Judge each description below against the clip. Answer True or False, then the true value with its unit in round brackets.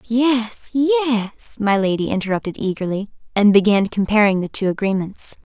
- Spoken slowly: True (130 wpm)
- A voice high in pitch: True (215 Hz)